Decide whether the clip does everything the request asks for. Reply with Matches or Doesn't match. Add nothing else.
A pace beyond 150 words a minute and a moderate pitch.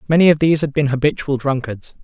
Matches